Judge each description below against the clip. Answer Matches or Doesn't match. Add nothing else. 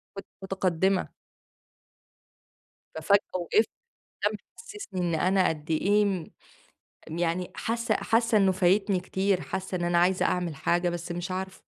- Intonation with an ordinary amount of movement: Doesn't match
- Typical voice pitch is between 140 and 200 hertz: Matches